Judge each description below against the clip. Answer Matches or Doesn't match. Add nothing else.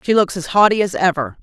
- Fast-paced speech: Matches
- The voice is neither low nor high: Matches